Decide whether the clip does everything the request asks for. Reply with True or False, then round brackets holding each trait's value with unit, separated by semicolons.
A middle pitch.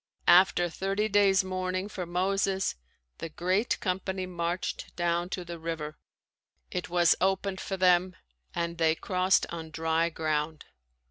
True (180 Hz)